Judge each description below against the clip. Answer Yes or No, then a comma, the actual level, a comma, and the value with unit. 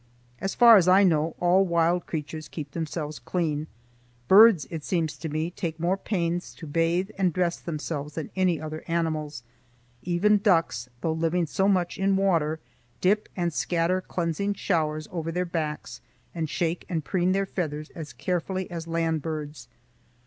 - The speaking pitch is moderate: Yes, medium, 170 Hz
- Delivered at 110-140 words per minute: No, average, 165 wpm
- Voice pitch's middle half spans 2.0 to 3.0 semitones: Yes, average, 2.7 semitones